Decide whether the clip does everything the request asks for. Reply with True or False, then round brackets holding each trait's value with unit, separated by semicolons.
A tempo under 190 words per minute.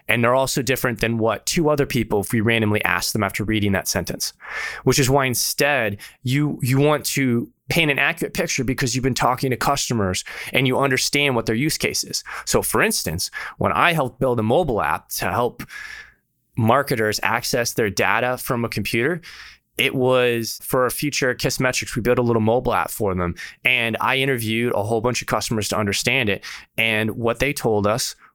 False (200 wpm)